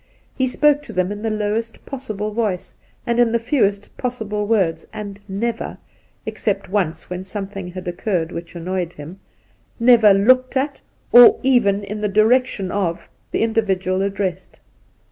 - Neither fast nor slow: Yes, average, 160 wpm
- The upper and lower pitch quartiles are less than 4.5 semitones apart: Yes, average, 3.7 semitones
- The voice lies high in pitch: Yes, high, 205 Hz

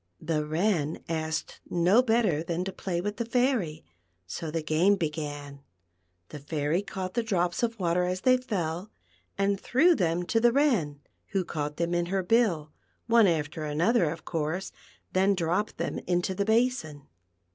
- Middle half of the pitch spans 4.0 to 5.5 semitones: Yes, average, 5.1 semitones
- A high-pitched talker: No, medium, 175 Hz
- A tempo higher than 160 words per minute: Yes, average, 170 wpm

